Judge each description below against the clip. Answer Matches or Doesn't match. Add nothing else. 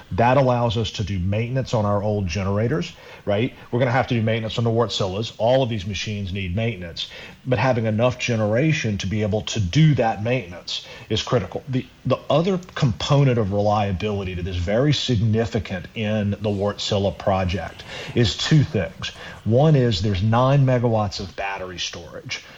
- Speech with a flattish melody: Doesn't match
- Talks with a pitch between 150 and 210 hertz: Doesn't match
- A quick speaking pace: Doesn't match